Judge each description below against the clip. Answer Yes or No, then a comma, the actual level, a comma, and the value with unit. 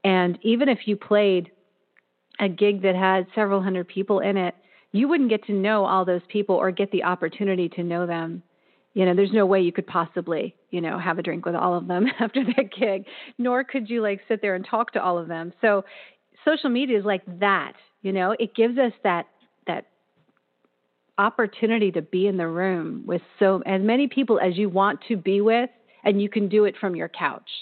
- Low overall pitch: No, high, 195 Hz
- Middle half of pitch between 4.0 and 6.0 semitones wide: No, average, 3.4 semitones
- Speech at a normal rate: No, fast, 215 wpm